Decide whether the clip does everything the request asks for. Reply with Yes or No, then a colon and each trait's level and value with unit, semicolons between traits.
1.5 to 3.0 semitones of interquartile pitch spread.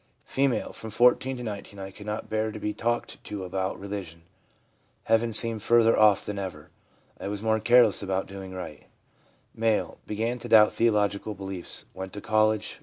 Yes: narrow, 2.4 semitones